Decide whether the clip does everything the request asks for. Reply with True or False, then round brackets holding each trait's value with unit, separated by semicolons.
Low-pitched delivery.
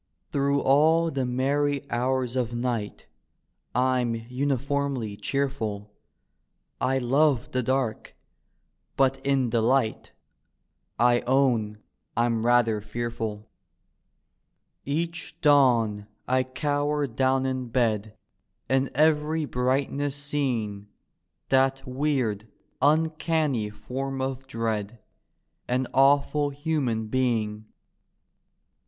True (130 Hz)